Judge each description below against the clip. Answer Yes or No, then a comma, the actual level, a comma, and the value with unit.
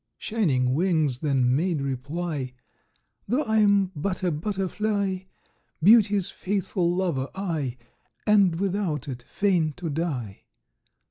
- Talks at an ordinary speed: No, slow, 110 wpm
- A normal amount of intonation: No, wide, 5.8 semitones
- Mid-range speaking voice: Yes, medium, 175 Hz